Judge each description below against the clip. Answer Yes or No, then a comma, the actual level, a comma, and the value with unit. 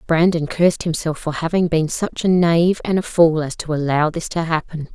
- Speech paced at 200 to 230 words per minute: Yes, fast, 205 wpm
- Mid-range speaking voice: Yes, medium, 165 Hz